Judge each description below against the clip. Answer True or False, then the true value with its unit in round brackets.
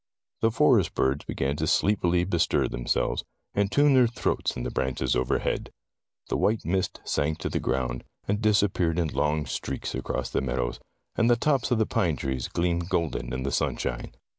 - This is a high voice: False (85 Hz)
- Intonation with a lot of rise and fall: True (7.5 semitones)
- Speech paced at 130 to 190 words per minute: True (180 wpm)